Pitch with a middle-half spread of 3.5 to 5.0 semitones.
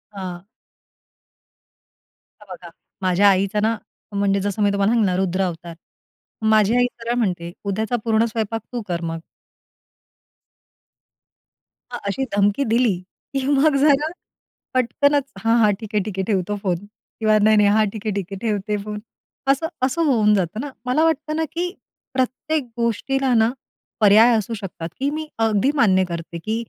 Yes: average, 3.9 semitones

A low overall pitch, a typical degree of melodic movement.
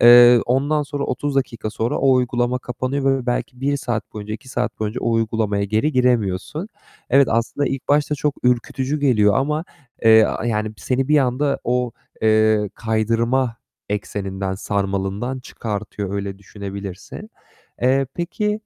Yes: low, 120 Hz; average, 4.0 semitones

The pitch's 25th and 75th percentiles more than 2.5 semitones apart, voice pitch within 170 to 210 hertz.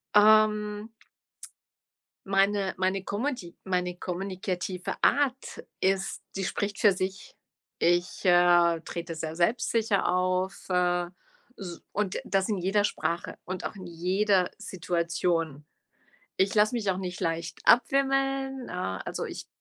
Yes: average, 2.9 semitones; high, 190 Hz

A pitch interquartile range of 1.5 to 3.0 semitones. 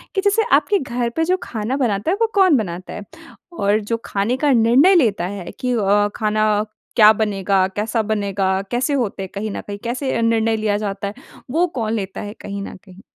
No: average, 4.2 semitones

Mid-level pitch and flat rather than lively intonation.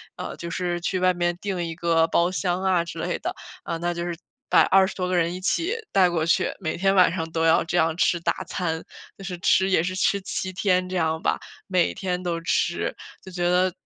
Yes: medium, 180 Hz; narrow, 1.7 semitones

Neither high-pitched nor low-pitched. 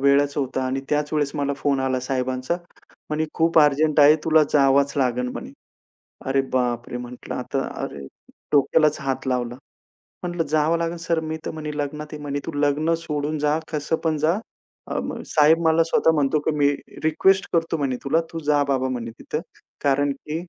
Yes: medium, 145 Hz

